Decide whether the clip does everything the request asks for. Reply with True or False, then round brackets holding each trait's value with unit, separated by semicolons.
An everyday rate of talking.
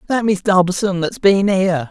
True (190 wpm)